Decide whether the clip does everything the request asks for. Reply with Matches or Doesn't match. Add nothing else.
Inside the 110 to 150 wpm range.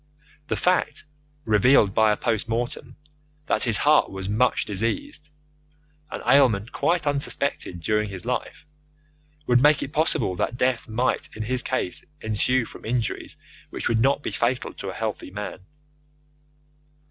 Matches